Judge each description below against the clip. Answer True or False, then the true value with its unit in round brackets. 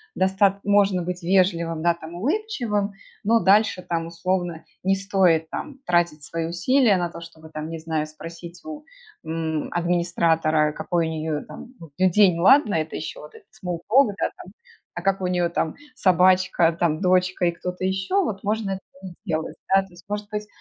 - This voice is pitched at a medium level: True (180 Hz)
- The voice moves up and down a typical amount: True (3.0 semitones)